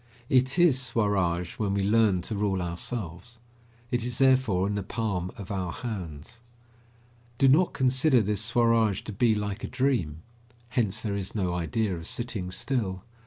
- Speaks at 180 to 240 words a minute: No, average, 165 wpm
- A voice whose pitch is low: Yes, low, 105 Hz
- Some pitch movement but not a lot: Yes, average, 4.7 semitones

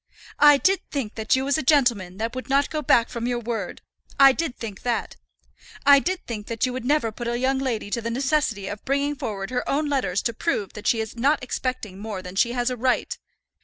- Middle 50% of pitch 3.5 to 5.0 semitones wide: Yes, average, 3.8 semitones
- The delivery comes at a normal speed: No, fast, 235 wpm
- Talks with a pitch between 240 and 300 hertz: Yes, high, 245 Hz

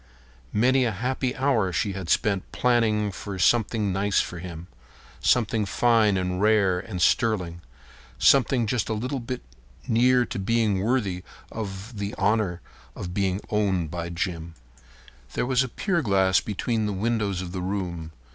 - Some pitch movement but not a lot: Yes, average, 4.1 semitones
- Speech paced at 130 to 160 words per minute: Yes, average, 150 wpm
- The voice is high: No, low, 100 Hz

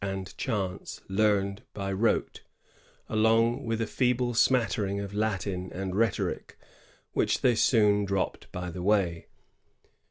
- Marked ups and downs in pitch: No, average, 2.8 semitones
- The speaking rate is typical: No, slow, 125 wpm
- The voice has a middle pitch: No, low, 105 Hz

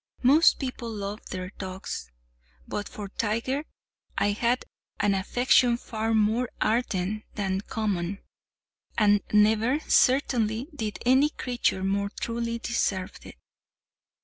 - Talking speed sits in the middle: No, slow, 110 wpm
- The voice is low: No, high, 215 Hz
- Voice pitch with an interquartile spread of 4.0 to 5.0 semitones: No, average, 3.5 semitones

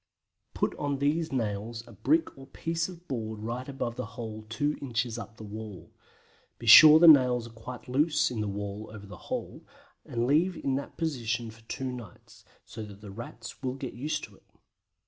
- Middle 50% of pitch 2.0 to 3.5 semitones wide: No, average, 4.4 semitones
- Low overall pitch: Yes, low, 120 Hz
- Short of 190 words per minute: No, average, 195 wpm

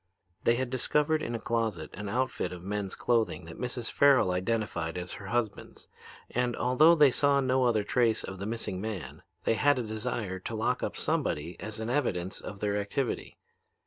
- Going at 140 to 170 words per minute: No, average, 185 wpm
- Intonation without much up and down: No, average, 4.2 semitones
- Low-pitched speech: Yes, low, 110 Hz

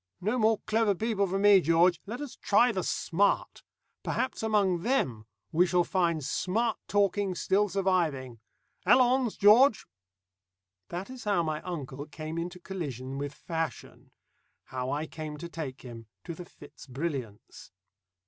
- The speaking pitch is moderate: Yes, medium, 180 Hz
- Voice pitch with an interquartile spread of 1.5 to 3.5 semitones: No, average, 5.2 semitones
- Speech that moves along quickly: No, average, 145 wpm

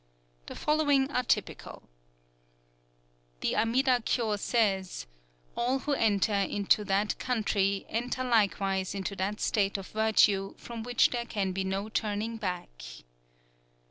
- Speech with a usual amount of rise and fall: Yes, average, 3.4 semitones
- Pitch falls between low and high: No, high, 215 Hz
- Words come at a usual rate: No, slow, 125 wpm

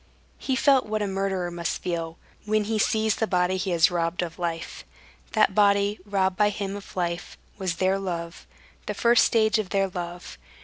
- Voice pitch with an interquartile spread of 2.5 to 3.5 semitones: Yes, average, 3.2 semitones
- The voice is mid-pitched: No, high, 195 Hz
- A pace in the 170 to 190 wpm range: Yes, average, 185 wpm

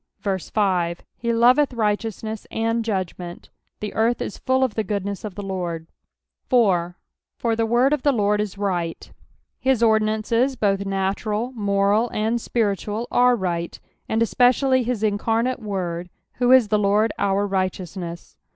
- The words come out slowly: No, average, 150 wpm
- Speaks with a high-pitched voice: Yes, high, 210 Hz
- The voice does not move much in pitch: No, average, 3.3 semitones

